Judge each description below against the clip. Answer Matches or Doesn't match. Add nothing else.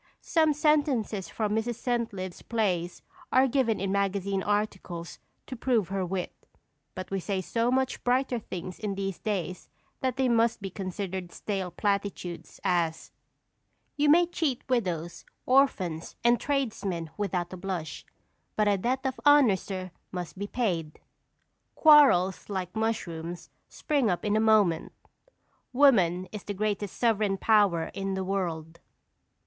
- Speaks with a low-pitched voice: Doesn't match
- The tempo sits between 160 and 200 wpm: Doesn't match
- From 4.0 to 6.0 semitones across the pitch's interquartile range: Matches